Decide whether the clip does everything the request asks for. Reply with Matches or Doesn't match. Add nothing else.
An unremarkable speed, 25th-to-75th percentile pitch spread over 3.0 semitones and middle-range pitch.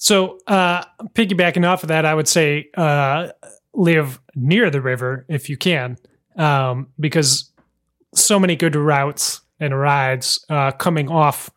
Matches